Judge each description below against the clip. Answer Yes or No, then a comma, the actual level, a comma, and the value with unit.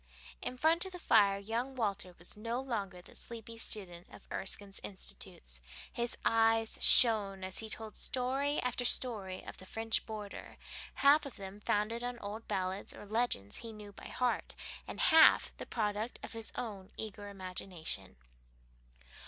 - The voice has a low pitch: No, high, 215 Hz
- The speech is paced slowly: No, average, 160 wpm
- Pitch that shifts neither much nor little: Yes, average, 3.3 semitones